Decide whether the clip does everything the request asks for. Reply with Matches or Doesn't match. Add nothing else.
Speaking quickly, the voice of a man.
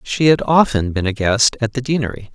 Matches